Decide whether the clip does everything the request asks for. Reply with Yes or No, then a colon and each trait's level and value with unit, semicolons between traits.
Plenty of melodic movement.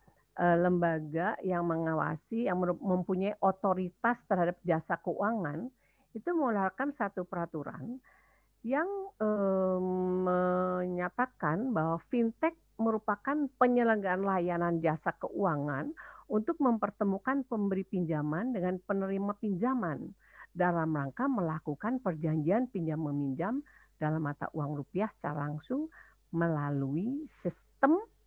Yes: wide, 5.7 semitones